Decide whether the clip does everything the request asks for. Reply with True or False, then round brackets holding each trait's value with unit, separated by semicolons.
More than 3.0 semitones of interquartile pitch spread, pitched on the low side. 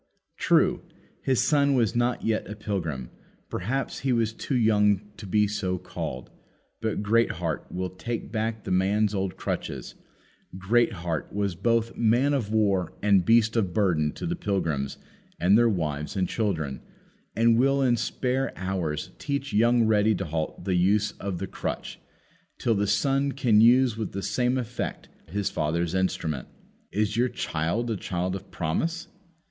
True (4.4 semitones; 105 Hz)